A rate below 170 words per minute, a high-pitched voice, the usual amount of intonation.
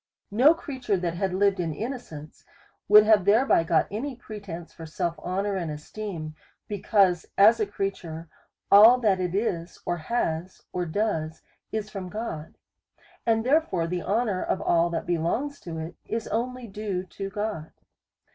Yes: average, 155 wpm; high, 195 Hz; average, 4.4 semitones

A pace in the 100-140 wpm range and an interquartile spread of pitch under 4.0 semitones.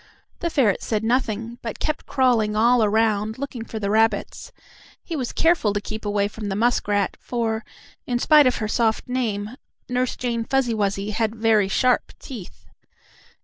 No: average, 165 wpm; average, 2.9 semitones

